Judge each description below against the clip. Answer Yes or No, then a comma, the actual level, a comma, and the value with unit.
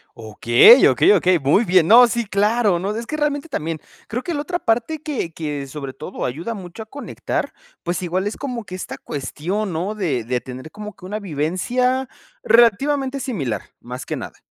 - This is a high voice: Yes, high, 200 Hz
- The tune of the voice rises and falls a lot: Yes, wide, 7.5 semitones